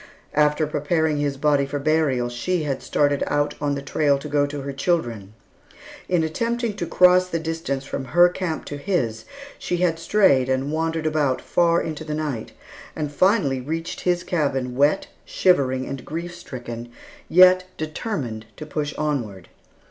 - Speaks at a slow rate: No, average, 165 wpm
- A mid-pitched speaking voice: Yes, medium, 150 Hz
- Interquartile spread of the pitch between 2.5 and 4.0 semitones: Yes, average, 3.5 semitones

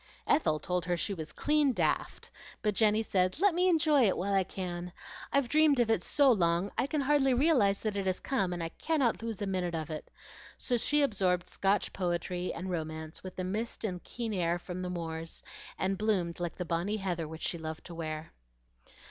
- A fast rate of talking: Yes, fast, 210 wpm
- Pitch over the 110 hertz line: Yes, high, 190 Hz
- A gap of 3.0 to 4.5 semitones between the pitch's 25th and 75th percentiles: No, average, 5.2 semitones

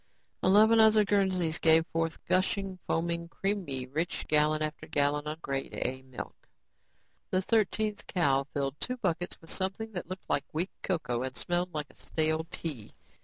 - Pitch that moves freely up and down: No, average, 4.4 semitones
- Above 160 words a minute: No, average, 155 wpm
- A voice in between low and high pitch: Yes, medium, 165 Hz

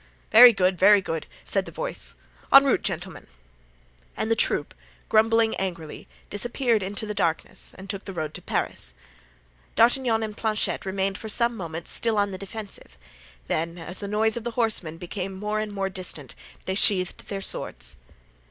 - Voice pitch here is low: No, high, 200 Hz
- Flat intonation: No, average, 3.4 semitones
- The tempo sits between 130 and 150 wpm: No, average, 170 wpm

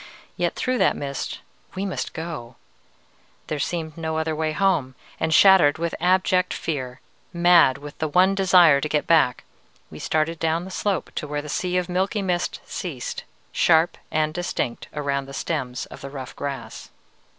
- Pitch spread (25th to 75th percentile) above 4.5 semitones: No, average, 3.7 semitones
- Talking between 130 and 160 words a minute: No, average, 170 wpm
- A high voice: No, medium, 160 Hz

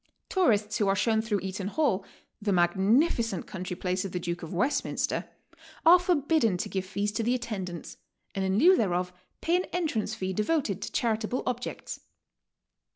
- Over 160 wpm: Yes, average, 170 wpm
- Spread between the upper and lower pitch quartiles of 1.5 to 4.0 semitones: No, average, 4.9 semitones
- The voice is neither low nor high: No, high, 210 Hz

